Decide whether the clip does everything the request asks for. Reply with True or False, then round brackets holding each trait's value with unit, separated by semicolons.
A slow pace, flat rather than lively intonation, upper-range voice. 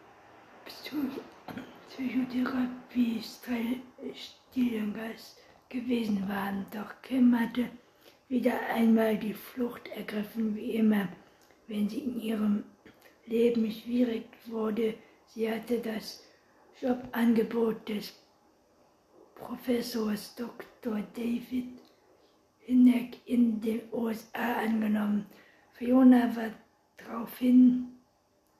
True (80 wpm; 2.1 semitones; 230 Hz)